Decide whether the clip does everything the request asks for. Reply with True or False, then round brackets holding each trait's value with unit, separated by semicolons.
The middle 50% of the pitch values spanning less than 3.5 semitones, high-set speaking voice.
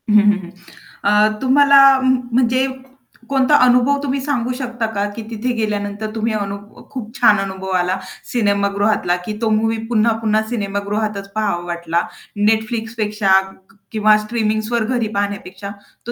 True (3.0 semitones; 215 Hz)